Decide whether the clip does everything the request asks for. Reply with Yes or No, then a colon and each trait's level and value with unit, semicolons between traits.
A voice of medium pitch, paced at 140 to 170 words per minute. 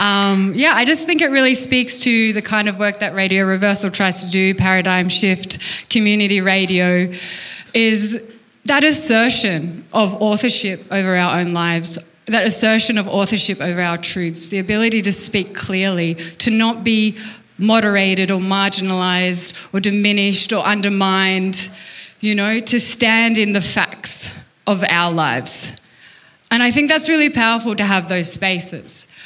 No: high, 200 Hz; average, 150 wpm